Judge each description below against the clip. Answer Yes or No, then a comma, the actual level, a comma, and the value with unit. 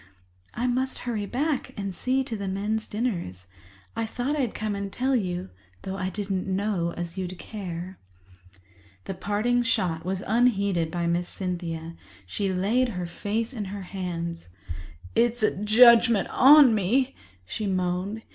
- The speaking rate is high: No, average, 150 wpm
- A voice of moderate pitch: No, high, 200 Hz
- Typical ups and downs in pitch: Yes, average, 4.4 semitones